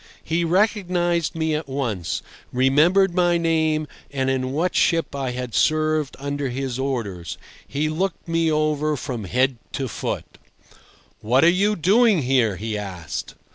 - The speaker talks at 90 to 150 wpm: Yes, average, 145 wpm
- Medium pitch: Yes, medium, 150 Hz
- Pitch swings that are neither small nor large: Yes, average, 4.6 semitones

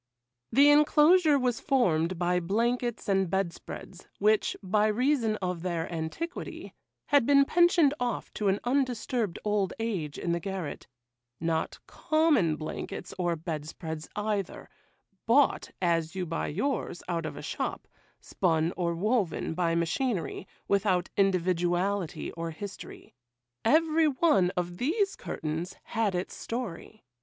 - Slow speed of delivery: Yes, slow, 125 wpm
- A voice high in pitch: Yes, high, 195 Hz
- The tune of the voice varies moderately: No, wide, 6.6 semitones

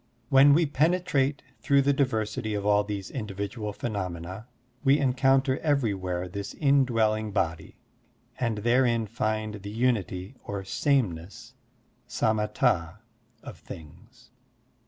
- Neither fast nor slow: No, slow, 115 wpm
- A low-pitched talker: Yes, low, 110 Hz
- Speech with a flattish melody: No, average, 4.9 semitones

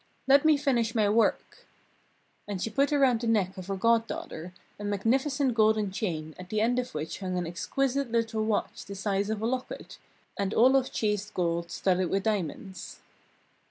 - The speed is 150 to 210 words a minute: Yes, average, 180 wpm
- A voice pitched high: Yes, high, 215 Hz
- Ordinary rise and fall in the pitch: Yes, average, 4.1 semitones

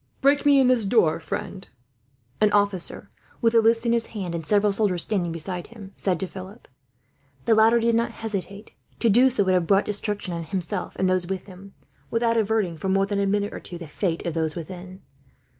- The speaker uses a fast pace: Yes, fast, 210 wpm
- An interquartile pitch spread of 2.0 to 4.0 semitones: Yes, average, 3.7 semitones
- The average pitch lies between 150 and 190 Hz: No, high, 200 Hz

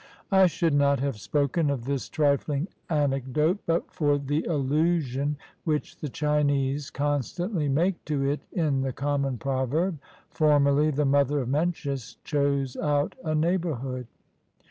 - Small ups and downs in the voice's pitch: Yes, narrow, 2.2 semitones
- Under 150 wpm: Yes, average, 140 wpm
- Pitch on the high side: No, medium, 145 Hz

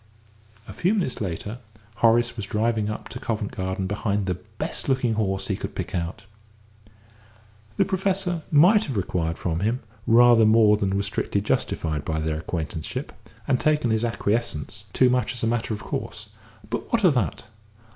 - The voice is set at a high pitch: No, low, 110 Hz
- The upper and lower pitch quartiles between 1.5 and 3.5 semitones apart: No, average, 4.2 semitones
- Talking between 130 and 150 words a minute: No, average, 170 wpm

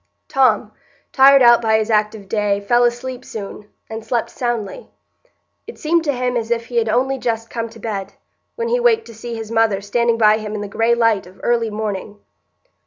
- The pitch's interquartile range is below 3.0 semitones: Yes, narrow, 2.4 semitones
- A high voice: Yes, high, 230 Hz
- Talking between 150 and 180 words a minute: No, average, 200 wpm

